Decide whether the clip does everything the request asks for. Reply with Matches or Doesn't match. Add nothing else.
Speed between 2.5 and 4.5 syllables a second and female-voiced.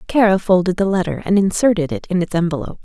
Doesn't match